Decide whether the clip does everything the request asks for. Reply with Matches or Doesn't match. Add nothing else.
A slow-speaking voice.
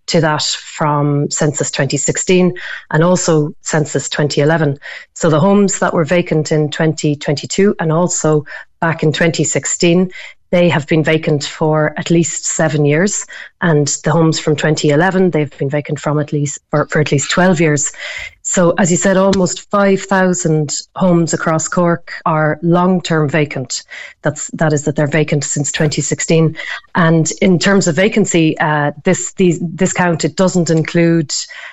Doesn't match